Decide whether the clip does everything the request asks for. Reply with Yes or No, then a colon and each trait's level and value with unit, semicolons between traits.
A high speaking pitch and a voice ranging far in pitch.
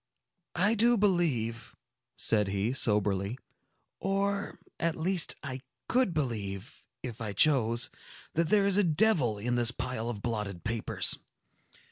No: low, 125 Hz; wide, 8.5 semitones